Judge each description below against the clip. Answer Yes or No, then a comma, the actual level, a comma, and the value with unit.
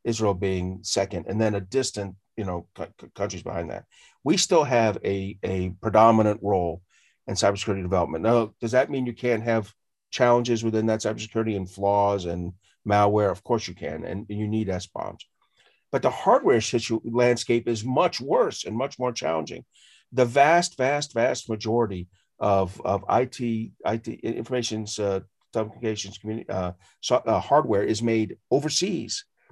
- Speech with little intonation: No, average, 3.2 semitones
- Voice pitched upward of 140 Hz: No, low, 110 Hz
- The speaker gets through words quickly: No, average, 160 wpm